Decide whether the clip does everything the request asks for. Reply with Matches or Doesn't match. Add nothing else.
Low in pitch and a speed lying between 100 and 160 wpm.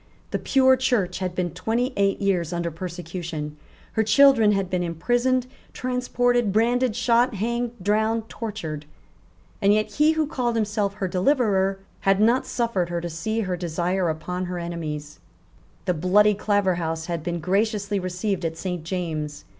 Doesn't match